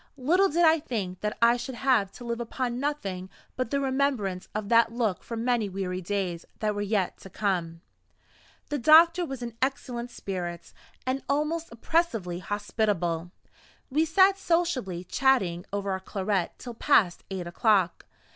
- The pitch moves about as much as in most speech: No, wide, 6.1 semitones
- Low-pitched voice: No, high, 230 Hz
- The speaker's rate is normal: Yes, average, 155 wpm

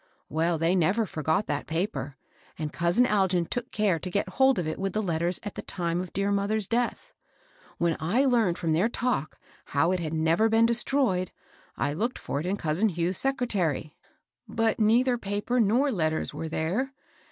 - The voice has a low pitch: No, high, 190 Hz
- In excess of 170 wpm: Yes, average, 190 wpm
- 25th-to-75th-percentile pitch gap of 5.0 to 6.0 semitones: Yes, wide, 5.5 semitones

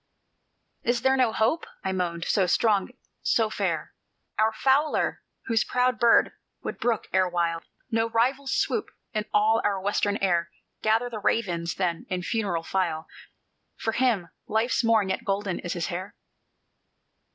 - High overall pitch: Yes, high, 215 Hz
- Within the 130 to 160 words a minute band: Yes, average, 145 wpm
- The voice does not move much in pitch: No, average, 3.9 semitones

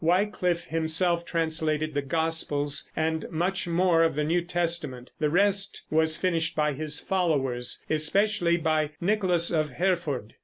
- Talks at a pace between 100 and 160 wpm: Yes, average, 140 wpm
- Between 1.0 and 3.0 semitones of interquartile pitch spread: Yes, narrow, 2.4 semitones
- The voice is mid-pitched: Yes, medium, 165 Hz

